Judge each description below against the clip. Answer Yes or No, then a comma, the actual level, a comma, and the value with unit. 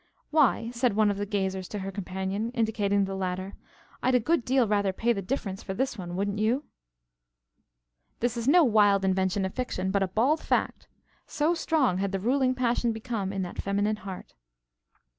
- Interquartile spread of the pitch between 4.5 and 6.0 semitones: No, average, 4.1 semitones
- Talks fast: No, average, 185 wpm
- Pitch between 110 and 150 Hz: No, high, 205 Hz